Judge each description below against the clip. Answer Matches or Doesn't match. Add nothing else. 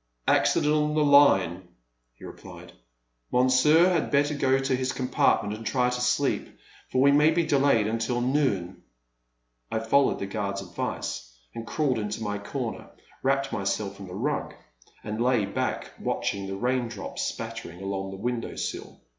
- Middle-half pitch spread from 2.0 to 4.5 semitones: Doesn't match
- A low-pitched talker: Matches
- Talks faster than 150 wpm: Matches